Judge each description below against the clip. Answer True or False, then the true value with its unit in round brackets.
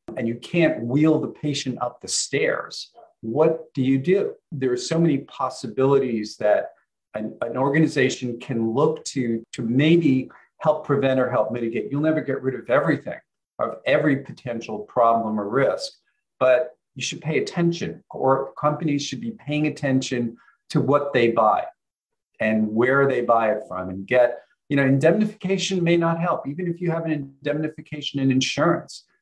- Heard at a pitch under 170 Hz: True (140 Hz)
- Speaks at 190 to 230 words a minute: False (170 wpm)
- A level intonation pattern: False (4.2 semitones)